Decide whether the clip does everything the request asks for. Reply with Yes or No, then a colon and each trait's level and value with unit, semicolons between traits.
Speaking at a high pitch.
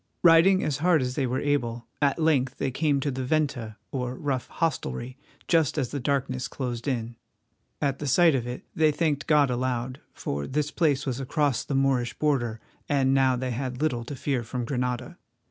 No: low, 135 Hz